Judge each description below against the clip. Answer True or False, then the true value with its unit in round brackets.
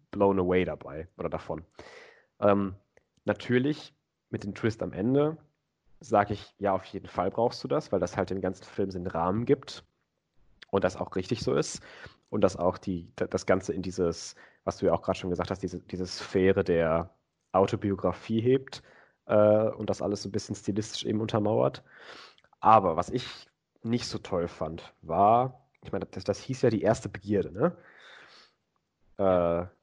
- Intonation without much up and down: False (3.5 semitones)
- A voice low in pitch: True (100 Hz)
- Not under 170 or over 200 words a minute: True (175 wpm)